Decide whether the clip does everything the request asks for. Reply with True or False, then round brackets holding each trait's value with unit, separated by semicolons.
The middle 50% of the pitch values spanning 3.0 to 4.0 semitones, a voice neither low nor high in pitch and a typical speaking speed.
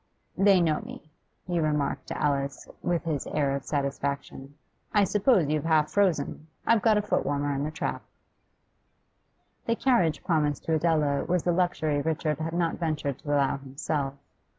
True (3.5 semitones; 155 Hz; 165 wpm)